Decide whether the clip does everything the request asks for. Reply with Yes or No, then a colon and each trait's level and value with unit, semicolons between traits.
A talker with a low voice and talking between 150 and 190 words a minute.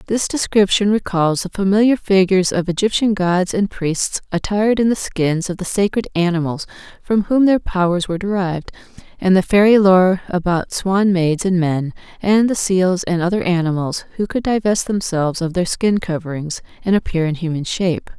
No: medium, 185 Hz; average, 175 wpm